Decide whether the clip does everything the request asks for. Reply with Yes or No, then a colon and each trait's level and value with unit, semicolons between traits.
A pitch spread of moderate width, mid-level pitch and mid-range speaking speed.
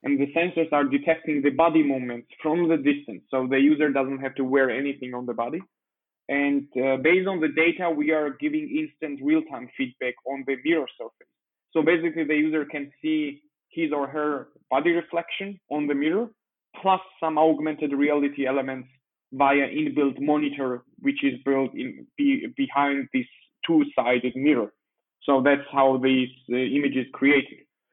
Yes: average, 3.9 semitones; medium, 150 Hz; average, 165 wpm